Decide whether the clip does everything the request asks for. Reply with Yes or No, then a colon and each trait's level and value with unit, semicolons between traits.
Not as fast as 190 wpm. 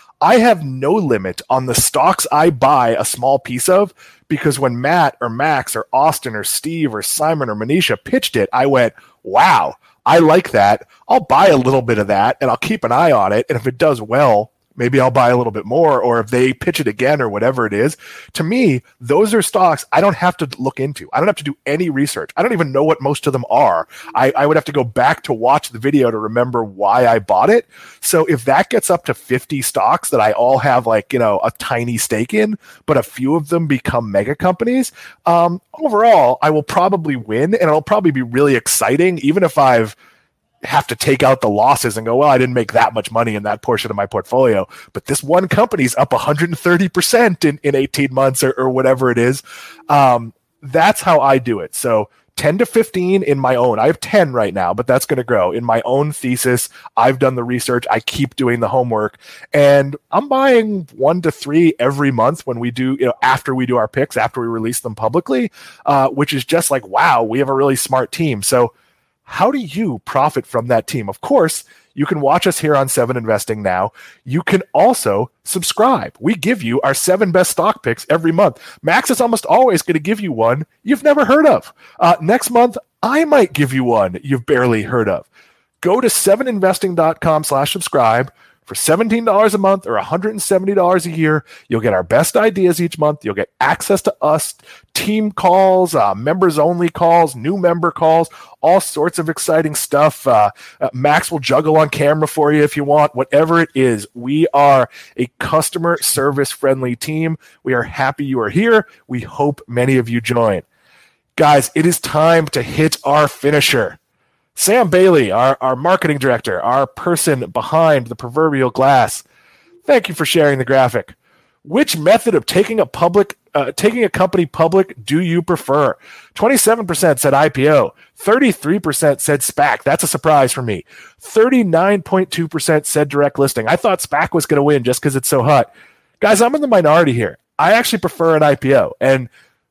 No: fast, 205 wpm